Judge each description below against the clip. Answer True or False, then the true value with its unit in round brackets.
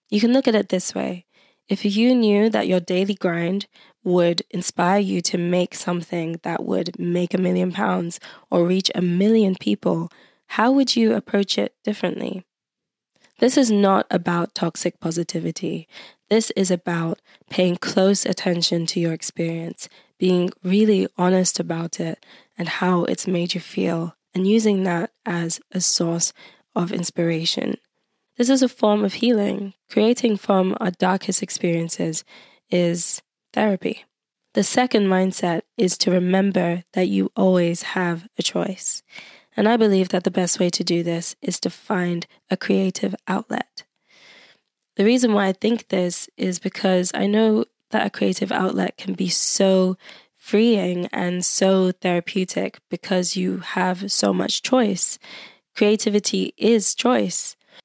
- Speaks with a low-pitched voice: False (185 Hz)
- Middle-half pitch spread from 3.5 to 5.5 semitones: False (2.9 semitones)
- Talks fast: False (145 wpm)